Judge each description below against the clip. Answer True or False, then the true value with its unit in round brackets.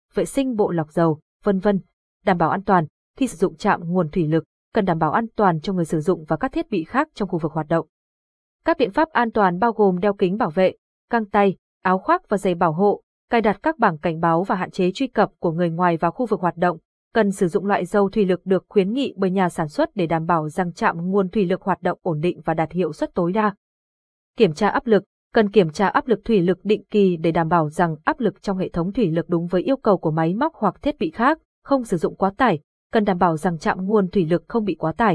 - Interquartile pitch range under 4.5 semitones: True (3.7 semitones)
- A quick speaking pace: True (270 wpm)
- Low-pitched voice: False (190 Hz)